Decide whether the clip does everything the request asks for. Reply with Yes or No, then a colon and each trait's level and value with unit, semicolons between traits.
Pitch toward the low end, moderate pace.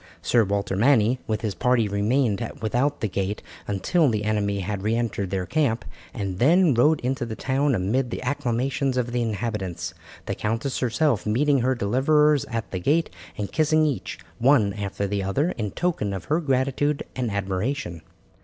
Yes: low, 115 Hz; average, 170 wpm